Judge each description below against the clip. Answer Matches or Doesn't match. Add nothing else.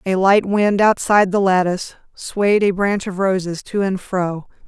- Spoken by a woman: Matches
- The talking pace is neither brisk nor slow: Matches